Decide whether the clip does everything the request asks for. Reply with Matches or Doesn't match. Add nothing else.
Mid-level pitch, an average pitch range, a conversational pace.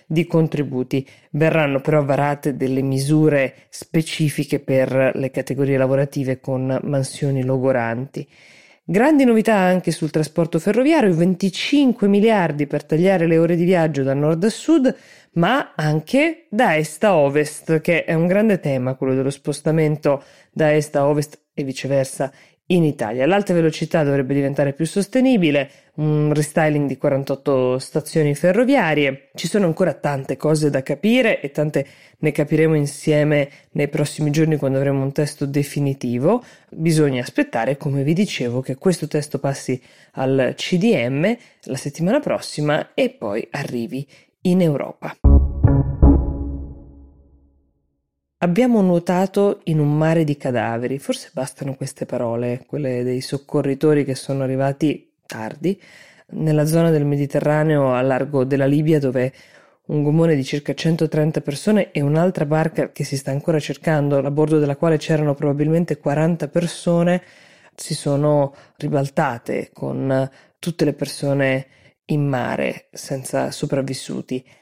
Matches